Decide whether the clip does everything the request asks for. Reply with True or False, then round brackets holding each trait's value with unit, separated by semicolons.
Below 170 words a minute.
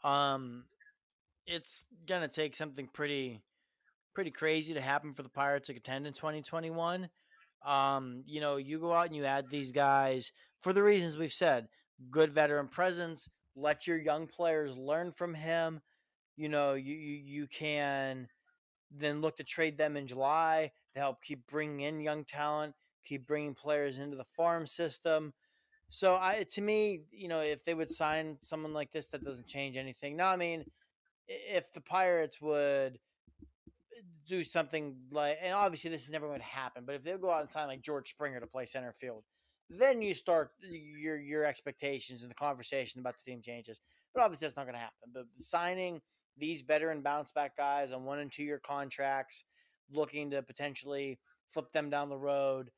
False (185 wpm)